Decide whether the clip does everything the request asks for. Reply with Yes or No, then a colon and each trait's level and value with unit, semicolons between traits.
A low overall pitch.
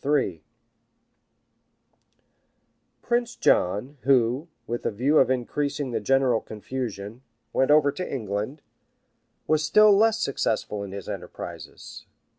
Yes: low, 130 Hz